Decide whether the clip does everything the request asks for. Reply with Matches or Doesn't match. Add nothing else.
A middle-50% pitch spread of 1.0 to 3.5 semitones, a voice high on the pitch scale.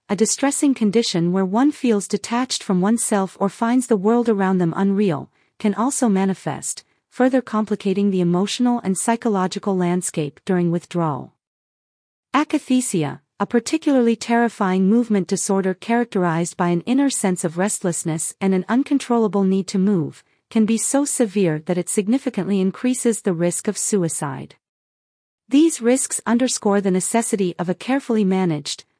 Doesn't match